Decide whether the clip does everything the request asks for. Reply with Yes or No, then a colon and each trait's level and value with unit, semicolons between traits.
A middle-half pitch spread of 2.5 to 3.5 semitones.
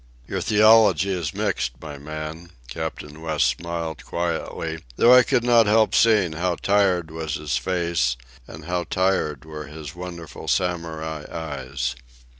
Yes: average, 3.1 semitones